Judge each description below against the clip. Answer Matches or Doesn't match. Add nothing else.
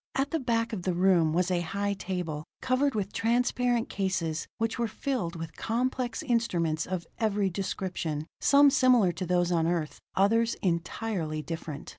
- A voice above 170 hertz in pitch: Matches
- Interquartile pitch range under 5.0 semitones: Doesn't match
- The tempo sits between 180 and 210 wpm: Doesn't match